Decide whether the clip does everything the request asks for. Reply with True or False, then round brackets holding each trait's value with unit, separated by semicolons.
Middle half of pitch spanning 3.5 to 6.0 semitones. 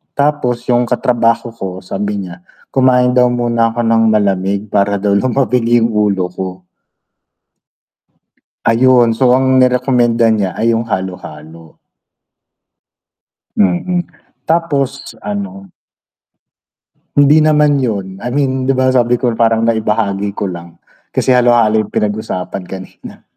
True (4.2 semitones)